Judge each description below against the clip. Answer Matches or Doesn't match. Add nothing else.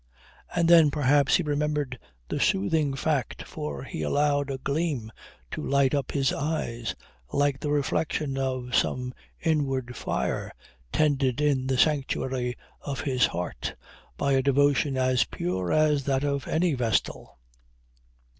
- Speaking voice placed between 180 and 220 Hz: Doesn't match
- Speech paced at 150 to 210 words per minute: Doesn't match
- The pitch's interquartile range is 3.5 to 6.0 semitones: Doesn't match